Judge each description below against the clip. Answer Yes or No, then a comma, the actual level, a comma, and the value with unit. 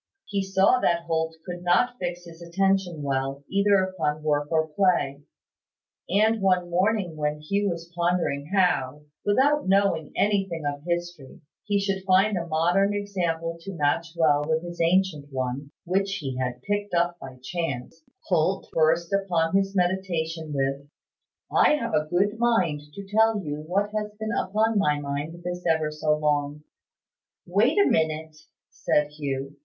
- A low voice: No, medium, 170 Hz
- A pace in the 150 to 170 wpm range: Yes, average, 155 wpm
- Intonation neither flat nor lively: Yes, average, 4.3 semitones